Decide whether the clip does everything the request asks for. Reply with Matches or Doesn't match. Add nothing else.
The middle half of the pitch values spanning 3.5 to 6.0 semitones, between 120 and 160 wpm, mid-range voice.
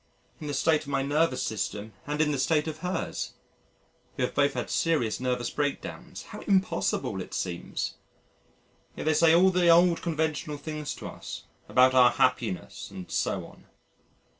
Doesn't match